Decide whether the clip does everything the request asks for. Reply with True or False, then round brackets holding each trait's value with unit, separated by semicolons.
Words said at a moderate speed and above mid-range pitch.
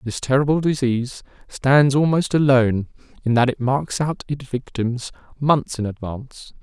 False (145 wpm; 130 Hz)